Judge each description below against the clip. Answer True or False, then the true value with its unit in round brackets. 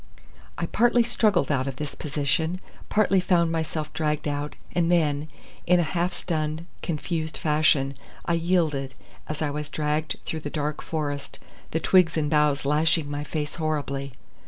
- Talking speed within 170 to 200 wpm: False (160 wpm)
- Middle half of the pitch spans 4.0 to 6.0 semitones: False (2.4 semitones)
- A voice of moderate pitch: True (155 Hz)